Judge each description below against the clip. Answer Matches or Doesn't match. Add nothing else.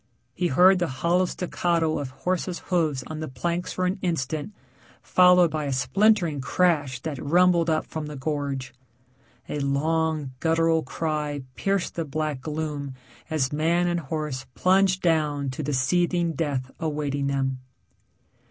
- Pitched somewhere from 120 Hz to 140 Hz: Doesn't match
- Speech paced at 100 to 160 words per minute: Matches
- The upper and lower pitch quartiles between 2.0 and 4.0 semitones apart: Matches